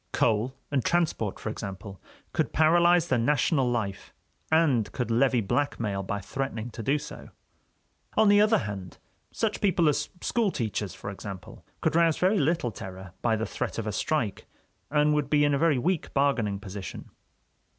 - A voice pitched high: No, low, 130 Hz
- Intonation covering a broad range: Yes, wide, 7.2 semitones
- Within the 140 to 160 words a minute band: No, average, 170 wpm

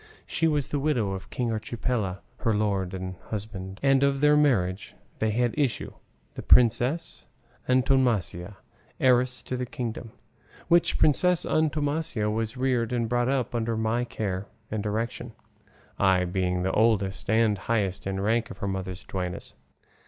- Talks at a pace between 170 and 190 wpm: No, average, 150 wpm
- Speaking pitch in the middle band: No, low, 115 Hz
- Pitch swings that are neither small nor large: Yes, average, 4.5 semitones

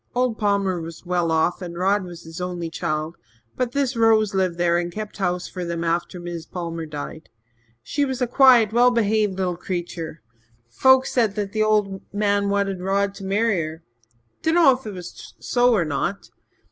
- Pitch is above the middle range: Yes, high, 195 Hz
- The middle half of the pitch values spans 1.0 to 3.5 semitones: No, average, 4.1 semitones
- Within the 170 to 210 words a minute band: Yes, average, 175 wpm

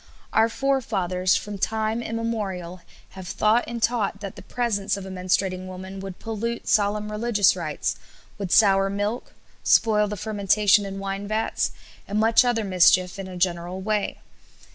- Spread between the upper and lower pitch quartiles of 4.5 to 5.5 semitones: No, average, 2.8 semitones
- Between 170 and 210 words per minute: No, average, 155 wpm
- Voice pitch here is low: No, high, 200 Hz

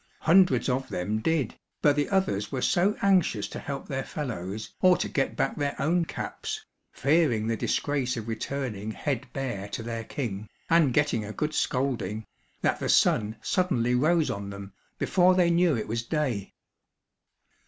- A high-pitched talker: No, low, 135 Hz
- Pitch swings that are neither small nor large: No, wide, 6.3 semitones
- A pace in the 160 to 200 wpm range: Yes, average, 165 wpm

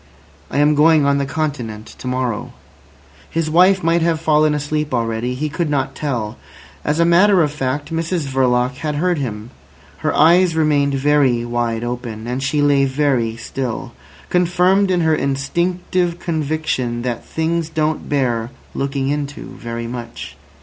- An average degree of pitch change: Yes, average, 4.3 semitones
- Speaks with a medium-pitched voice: Yes, medium, 145 Hz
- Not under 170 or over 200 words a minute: No, average, 155 wpm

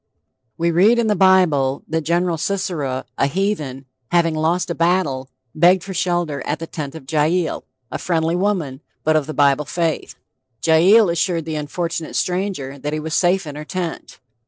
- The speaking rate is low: No, average, 175 wpm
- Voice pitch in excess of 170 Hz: No, medium, 165 Hz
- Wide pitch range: No, average, 3.3 semitones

